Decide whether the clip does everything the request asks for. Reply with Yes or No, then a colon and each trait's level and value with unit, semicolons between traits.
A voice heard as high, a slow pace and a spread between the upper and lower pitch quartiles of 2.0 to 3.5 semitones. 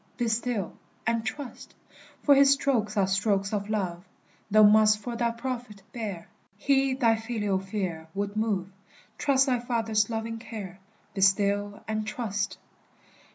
No: high, 215 Hz; average, 145 wpm; average, 2.9 semitones